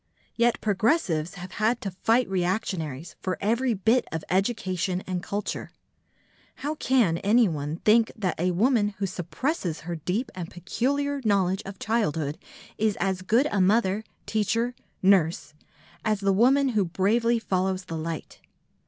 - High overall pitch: Yes, high, 195 Hz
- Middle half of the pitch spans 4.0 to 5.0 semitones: Yes, average, 4.3 semitones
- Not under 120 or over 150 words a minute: Yes, average, 145 wpm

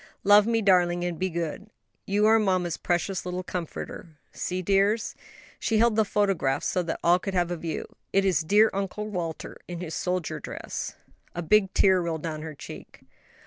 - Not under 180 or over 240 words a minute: Yes, average, 185 wpm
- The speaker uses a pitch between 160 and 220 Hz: Yes, medium, 185 Hz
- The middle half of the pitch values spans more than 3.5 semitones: No, average, 2.9 semitones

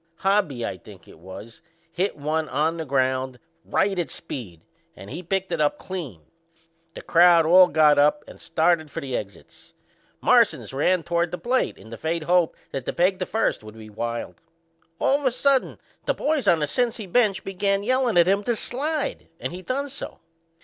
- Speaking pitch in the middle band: Yes, medium, 170 Hz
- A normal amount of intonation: No, wide, 6.4 semitones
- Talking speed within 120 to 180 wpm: No, average, 190 wpm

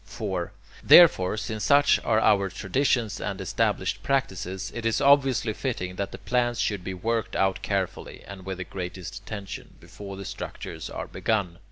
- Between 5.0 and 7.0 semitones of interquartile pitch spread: No, average, 3.7 semitones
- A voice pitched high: No, low, 100 Hz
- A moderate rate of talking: Yes, average, 165 wpm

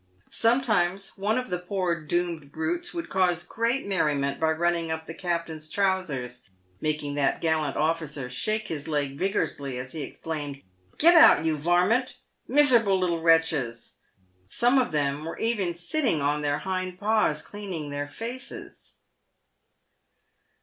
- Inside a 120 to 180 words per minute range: Yes, average, 150 wpm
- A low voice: No, medium, 170 Hz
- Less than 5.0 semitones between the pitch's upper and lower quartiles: No, average, 5.3 semitones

